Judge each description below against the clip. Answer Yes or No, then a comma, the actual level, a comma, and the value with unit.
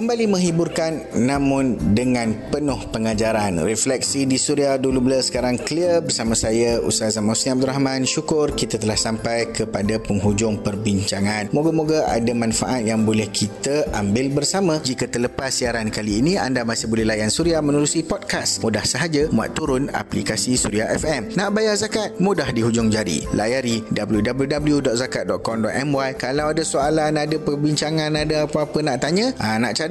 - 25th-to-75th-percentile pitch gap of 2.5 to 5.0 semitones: No, wide, 5.5 semitones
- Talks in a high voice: No, low, 130 Hz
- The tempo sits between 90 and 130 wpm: No, average, 145 wpm